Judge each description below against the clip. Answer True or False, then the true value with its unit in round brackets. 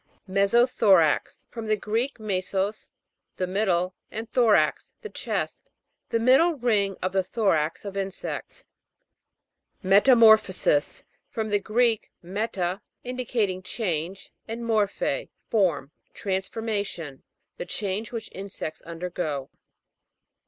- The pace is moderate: False (105 wpm)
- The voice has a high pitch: True (200 Hz)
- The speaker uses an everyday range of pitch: True (3.5 semitones)